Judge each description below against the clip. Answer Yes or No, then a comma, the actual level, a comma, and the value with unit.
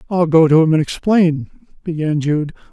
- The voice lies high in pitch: No, medium, 160 Hz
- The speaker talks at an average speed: Yes, average, 175 wpm